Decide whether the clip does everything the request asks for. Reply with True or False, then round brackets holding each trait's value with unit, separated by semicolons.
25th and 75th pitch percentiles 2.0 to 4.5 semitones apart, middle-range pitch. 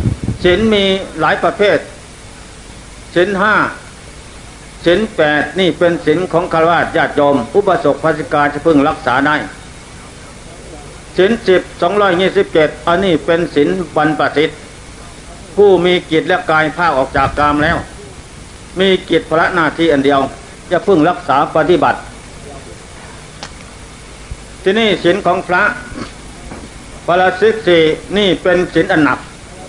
True (3.2 semitones; 165 Hz)